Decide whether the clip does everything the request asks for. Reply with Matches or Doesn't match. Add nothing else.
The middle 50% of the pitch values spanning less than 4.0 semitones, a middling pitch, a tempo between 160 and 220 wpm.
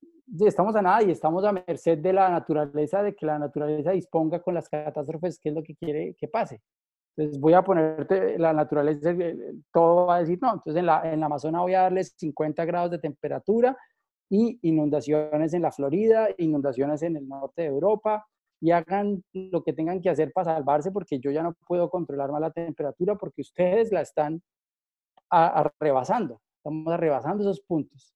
Matches